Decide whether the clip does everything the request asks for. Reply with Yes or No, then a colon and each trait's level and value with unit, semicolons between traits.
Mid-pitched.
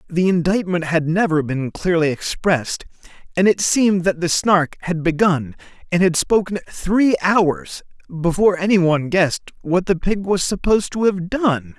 Yes: medium, 180 Hz